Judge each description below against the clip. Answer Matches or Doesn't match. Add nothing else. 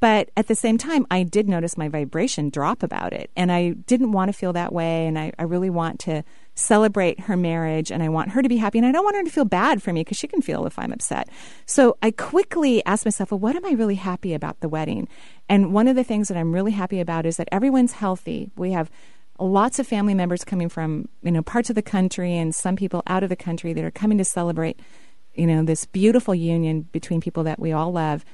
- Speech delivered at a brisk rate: Matches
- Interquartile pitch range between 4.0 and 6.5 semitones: Matches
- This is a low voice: Doesn't match